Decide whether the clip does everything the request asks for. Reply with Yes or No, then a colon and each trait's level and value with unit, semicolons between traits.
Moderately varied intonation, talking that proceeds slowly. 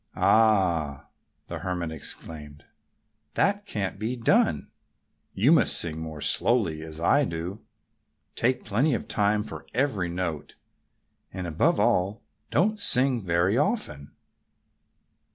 No: wide, 6.8 semitones; slow, 115 wpm